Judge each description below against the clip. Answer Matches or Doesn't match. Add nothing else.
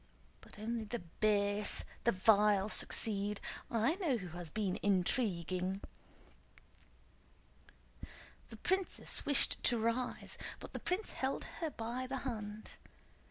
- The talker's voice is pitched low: Doesn't match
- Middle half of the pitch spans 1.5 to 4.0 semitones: Matches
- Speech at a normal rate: Doesn't match